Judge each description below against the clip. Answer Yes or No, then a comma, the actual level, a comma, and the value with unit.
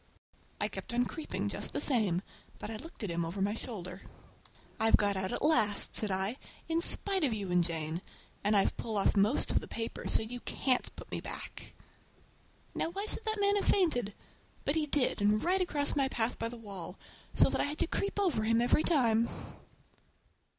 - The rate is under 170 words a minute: No, fast, 205 wpm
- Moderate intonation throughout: No, wide, 6.9 semitones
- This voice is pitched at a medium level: No, high, 230 Hz